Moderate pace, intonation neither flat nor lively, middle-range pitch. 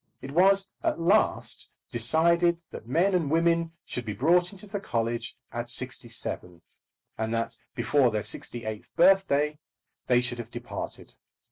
No: average, 150 wpm; wide, 6.8 semitones; medium, 150 Hz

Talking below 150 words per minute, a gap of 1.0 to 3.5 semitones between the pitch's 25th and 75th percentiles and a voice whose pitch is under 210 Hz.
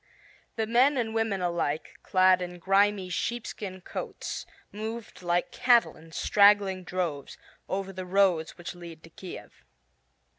Yes: slow, 135 wpm; average, 3.0 semitones; medium, 185 Hz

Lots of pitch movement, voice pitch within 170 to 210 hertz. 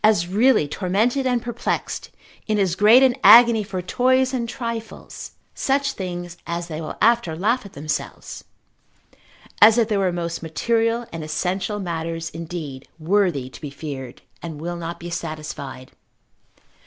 Yes: wide, 5.8 semitones; medium, 185 Hz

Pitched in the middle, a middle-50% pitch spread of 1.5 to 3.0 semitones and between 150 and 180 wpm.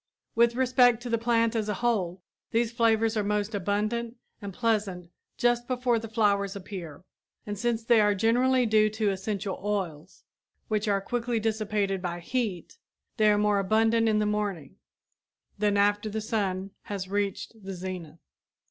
No: high, 210 Hz; narrow, 2.6 semitones; average, 160 wpm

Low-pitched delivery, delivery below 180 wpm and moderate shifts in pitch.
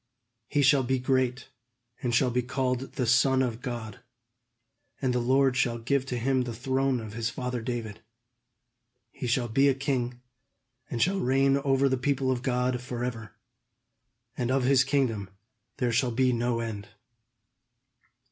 No: low, 125 Hz; average, 155 wpm; narrow, 1.9 semitones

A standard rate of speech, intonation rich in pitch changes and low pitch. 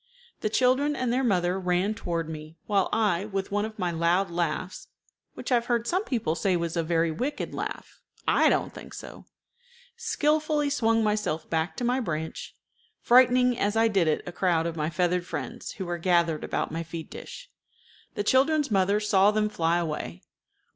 No: average, 185 wpm; wide, 5.9 semitones; high, 195 Hz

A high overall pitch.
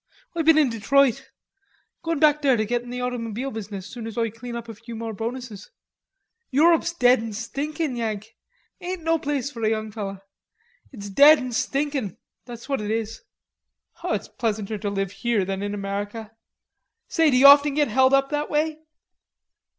Yes: high, 240 Hz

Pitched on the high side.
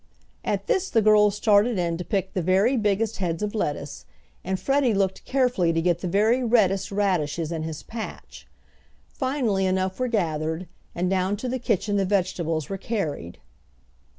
Yes: high, 195 Hz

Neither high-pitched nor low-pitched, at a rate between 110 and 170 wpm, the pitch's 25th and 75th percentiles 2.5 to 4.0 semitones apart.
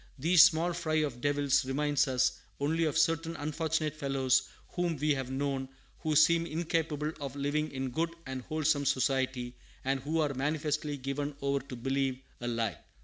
Yes: medium, 145 Hz; average, 165 wpm; average, 2.9 semitones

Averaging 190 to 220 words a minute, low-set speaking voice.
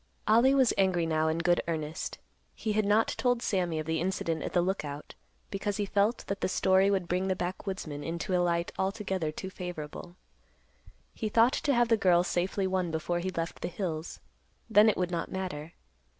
No: average, 195 wpm; medium, 185 Hz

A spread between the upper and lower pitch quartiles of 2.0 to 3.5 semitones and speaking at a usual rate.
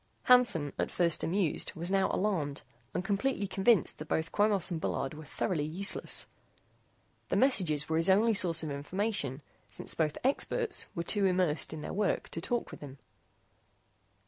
No: average, 4.8 semitones; average, 165 wpm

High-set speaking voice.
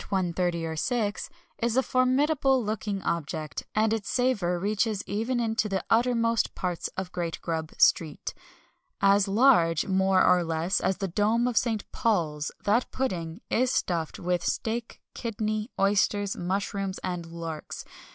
Yes: high, 200 Hz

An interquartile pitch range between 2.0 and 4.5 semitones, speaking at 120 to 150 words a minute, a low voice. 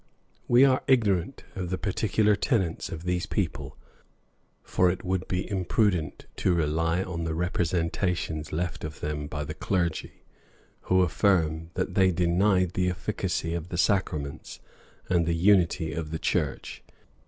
Yes: narrow, 2.5 semitones; average, 145 wpm; very low, 90 Hz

